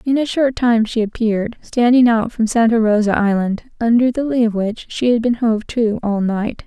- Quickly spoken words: Yes, fast, 215 wpm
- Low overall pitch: No, high, 230 Hz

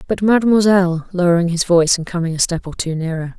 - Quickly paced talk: No, average, 195 wpm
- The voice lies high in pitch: No, medium, 175 Hz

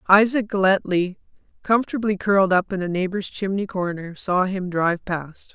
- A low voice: No, high, 190 Hz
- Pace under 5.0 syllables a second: No, 5.1 syllables/s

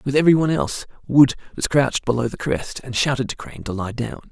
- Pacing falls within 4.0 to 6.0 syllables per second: No, 6.6 syllables/s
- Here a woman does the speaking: No, male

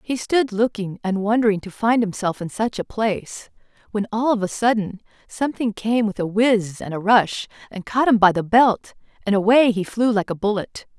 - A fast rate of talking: Yes, fast, 210 wpm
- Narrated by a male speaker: No, female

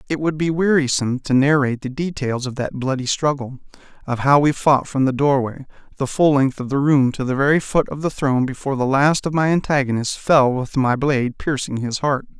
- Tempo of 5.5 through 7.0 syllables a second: Yes, 5.7 syllables/s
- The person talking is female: No, male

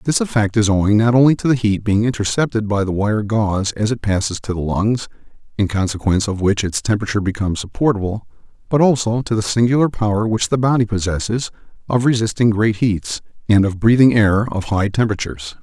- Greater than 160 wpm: Yes, average, 190 wpm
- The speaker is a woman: No, male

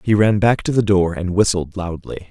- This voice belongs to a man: Yes, male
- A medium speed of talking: No, fast, 235 wpm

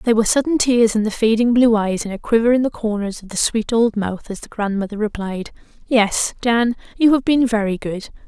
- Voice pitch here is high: Yes, high, 225 Hz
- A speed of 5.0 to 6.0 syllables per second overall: Yes, 5.5 syllables/s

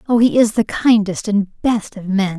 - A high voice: Yes, high, 210 Hz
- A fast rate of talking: Yes, fast, 225 wpm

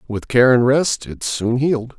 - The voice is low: Yes, low, 125 Hz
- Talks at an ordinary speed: No, fast, 210 wpm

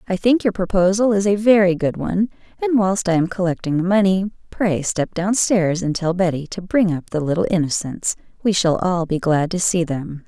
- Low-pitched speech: No, medium, 185 Hz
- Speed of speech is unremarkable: No, fast, 210 wpm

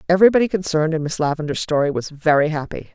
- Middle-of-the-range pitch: Yes, medium, 160 Hz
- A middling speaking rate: Yes, average, 185 wpm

